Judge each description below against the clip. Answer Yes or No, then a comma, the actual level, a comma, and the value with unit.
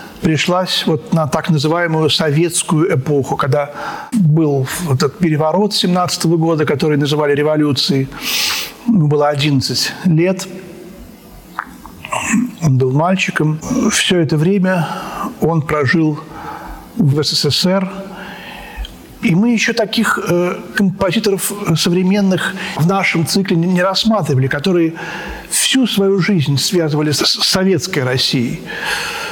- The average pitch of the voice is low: No, medium, 170 Hz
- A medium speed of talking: No, slow, 100 wpm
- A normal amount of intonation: Yes, average, 4.0 semitones